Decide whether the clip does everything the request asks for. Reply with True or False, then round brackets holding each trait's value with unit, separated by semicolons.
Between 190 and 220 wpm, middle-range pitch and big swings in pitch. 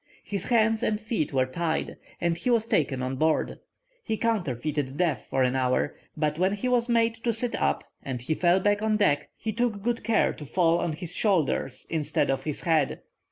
True (205 wpm; 175 Hz; 6.9 semitones)